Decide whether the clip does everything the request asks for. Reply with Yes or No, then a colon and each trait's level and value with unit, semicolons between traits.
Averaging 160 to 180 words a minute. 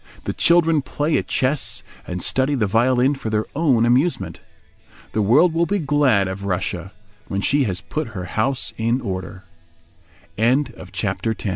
Yes: average, 165 wpm